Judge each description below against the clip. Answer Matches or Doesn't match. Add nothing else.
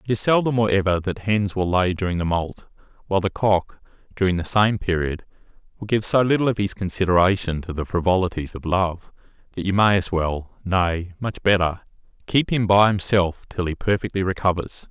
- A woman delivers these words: Doesn't match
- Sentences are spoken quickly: Doesn't match